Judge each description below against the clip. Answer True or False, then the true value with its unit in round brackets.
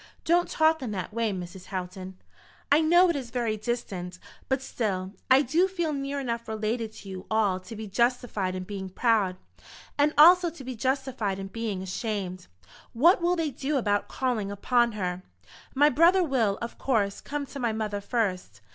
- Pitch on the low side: False (230 Hz)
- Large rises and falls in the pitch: True (5.8 semitones)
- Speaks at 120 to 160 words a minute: False (180 wpm)